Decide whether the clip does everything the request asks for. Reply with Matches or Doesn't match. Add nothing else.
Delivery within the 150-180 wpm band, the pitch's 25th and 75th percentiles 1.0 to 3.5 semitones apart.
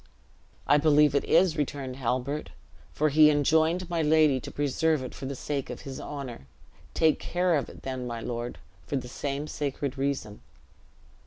Matches